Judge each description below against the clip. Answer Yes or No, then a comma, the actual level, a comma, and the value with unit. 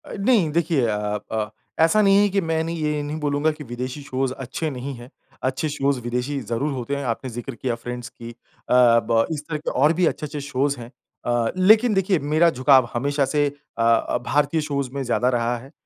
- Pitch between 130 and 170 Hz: Yes, medium, 140 Hz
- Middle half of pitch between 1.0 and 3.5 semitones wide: No, average, 4.1 semitones